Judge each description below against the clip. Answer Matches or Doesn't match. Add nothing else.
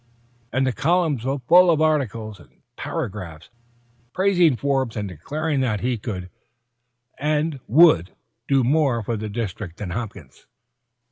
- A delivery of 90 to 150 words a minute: Matches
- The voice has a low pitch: Matches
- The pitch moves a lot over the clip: Matches